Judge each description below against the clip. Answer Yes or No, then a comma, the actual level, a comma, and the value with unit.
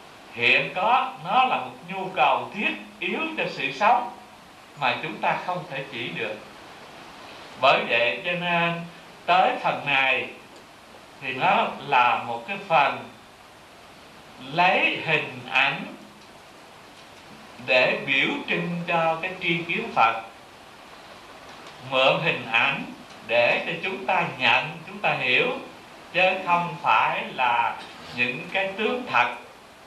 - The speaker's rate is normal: No, slow, 125 wpm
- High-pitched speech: No, medium, 175 Hz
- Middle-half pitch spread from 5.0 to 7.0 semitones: Yes, wide, 5.8 semitones